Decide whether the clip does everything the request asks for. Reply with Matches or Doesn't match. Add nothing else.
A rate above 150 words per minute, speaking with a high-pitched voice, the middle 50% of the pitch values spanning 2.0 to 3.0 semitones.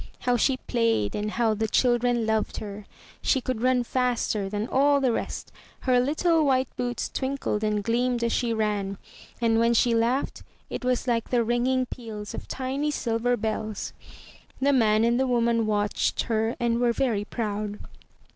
Matches